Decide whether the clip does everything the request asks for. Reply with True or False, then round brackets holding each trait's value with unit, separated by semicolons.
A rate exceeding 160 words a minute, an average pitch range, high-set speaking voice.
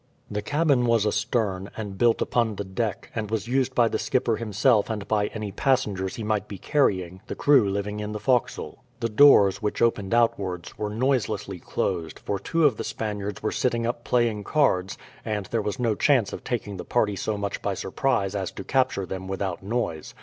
False (200 wpm; 3.3 semitones; 105 Hz)